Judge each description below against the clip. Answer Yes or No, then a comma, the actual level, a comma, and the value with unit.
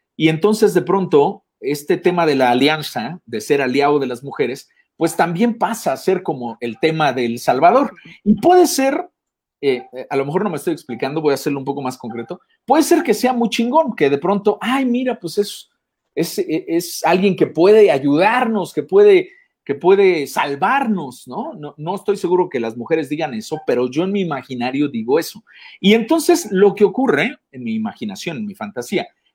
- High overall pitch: Yes, high, 195 Hz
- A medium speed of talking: No, fast, 195 wpm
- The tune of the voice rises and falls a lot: Yes, wide, 9.0 semitones